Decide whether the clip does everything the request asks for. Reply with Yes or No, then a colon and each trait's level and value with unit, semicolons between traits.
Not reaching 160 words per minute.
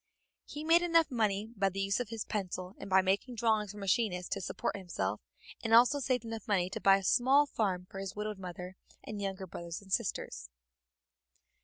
No: average, 195 wpm